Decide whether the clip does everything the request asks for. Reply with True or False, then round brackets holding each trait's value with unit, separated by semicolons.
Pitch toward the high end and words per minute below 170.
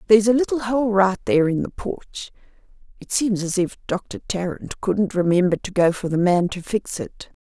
False (195 Hz; 200 wpm)